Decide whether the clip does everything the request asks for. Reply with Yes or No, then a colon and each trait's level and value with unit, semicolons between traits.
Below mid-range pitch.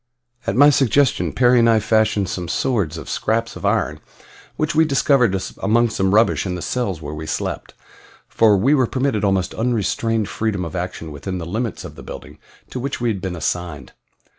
Yes: low, 110 Hz